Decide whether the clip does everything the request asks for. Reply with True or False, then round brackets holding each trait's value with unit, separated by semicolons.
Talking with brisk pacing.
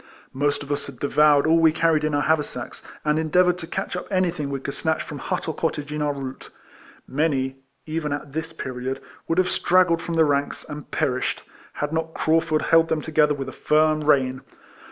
True (210 wpm)